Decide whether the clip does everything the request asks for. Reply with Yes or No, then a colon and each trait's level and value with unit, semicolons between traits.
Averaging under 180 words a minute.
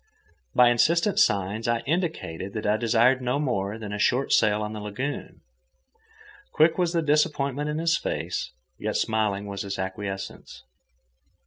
Yes: average, 150 wpm